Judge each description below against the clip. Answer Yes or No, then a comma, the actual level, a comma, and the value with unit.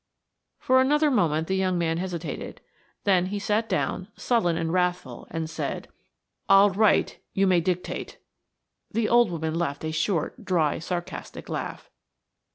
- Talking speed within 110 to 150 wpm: Yes, average, 140 wpm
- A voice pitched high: No, medium, 180 Hz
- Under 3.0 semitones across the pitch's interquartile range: No, average, 3.8 semitones